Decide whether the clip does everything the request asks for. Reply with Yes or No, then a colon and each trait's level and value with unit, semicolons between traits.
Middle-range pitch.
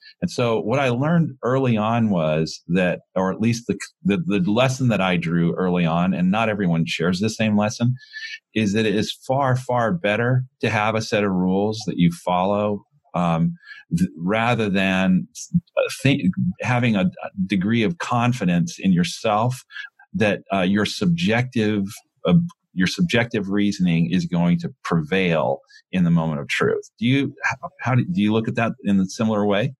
No: low, 115 Hz